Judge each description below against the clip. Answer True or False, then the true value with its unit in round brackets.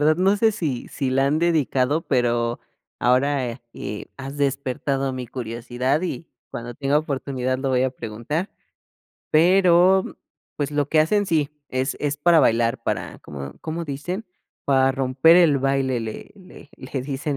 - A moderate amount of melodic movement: True (3.6 semitones)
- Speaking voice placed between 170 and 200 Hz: False (140 Hz)